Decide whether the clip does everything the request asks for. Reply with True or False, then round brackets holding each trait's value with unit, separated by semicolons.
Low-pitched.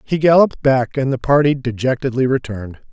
True (130 Hz)